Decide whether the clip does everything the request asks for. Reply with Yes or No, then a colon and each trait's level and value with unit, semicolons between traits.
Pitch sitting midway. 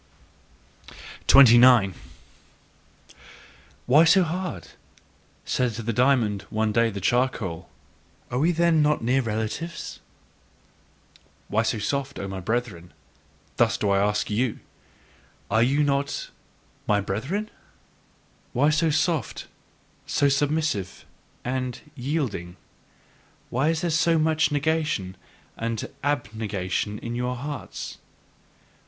No: low, 125 Hz